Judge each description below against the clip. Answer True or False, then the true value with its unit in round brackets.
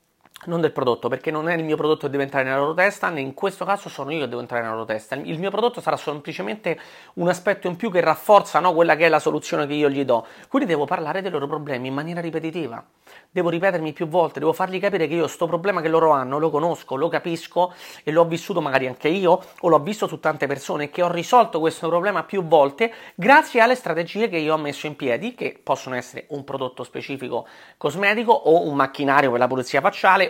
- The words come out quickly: True (230 wpm)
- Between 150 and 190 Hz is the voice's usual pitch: True (160 Hz)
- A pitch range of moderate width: True (3.9 semitones)